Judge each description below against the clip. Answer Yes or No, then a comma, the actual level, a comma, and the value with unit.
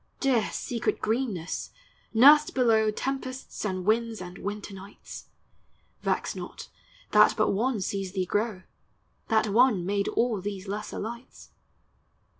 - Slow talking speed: Yes, slow, 125 wpm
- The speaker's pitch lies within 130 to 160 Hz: No, high, 215 Hz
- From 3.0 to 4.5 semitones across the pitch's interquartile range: Yes, average, 3.4 semitones